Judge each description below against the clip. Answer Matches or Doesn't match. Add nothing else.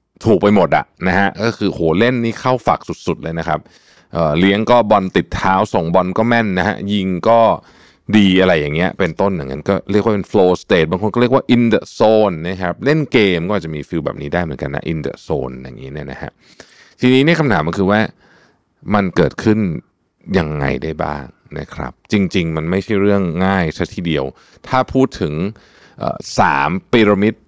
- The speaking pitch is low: Matches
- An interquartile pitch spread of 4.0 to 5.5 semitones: Matches